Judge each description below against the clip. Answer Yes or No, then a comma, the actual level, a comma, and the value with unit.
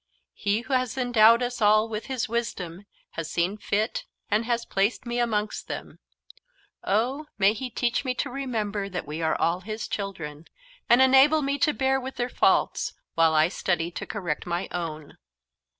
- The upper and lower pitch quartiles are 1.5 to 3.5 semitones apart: No, wide, 5.4 semitones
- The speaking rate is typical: Yes, average, 175 wpm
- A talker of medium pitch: No, high, 215 Hz